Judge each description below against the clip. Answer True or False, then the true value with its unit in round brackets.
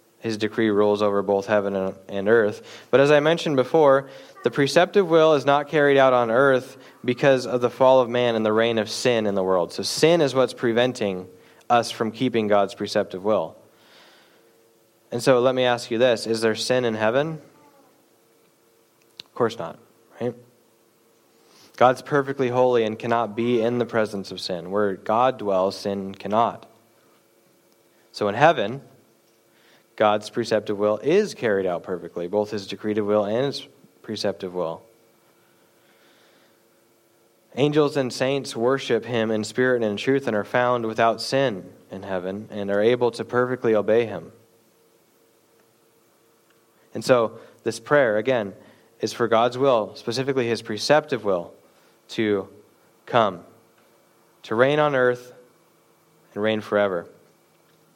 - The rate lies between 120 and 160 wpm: True (150 wpm)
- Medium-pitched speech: False (115 Hz)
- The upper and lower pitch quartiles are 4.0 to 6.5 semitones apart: False (3.4 semitones)